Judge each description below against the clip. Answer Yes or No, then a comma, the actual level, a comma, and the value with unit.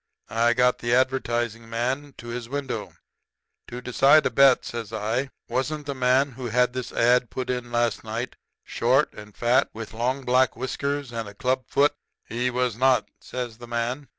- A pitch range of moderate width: No, narrow, 1.8 semitones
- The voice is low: Yes, low, 125 Hz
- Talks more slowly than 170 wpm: No, average, 180 wpm